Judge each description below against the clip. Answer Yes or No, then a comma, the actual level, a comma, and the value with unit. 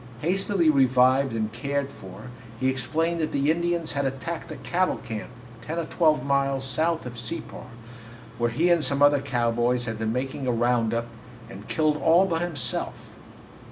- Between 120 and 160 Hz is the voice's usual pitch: Yes, medium, 140 Hz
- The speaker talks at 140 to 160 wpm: No, average, 170 wpm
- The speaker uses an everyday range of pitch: Yes, average, 4.9 semitones